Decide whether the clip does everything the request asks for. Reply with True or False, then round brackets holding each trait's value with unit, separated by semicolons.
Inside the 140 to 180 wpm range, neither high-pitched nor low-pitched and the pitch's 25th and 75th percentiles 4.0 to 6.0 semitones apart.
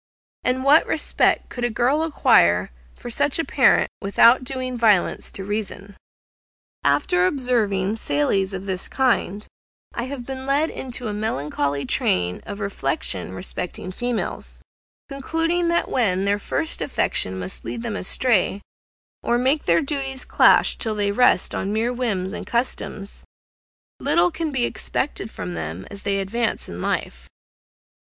False (145 wpm; 220 Hz; 5.5 semitones)